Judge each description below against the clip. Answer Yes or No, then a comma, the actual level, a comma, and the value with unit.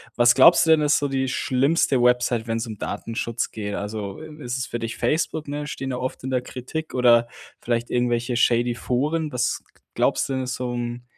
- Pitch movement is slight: Yes, narrow, 2.3 semitones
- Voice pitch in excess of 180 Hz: No, low, 125 Hz